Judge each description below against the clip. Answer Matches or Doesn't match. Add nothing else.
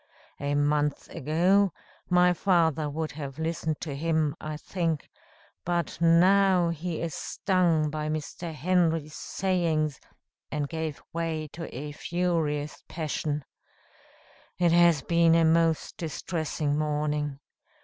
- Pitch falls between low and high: Matches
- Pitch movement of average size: Doesn't match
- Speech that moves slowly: Matches